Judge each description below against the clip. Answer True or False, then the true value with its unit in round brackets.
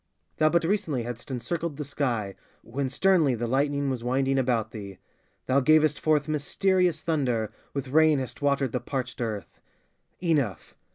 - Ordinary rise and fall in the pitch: True (4.1 semitones)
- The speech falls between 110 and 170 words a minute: True (155 wpm)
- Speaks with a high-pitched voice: False (140 Hz)